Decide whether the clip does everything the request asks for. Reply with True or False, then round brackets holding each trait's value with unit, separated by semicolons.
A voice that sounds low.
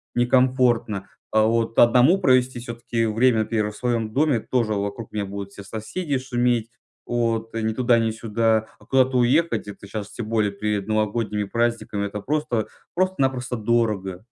True (115 Hz)